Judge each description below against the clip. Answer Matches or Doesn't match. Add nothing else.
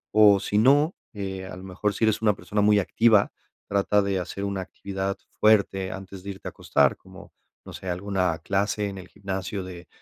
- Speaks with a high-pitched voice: Doesn't match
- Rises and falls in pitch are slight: Matches